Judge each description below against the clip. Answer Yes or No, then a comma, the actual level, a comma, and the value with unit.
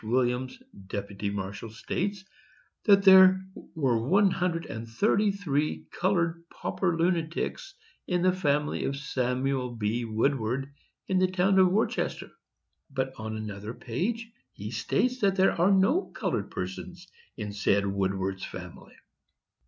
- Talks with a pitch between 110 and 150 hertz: Yes, medium, 140 Hz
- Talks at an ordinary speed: No, slow, 130 wpm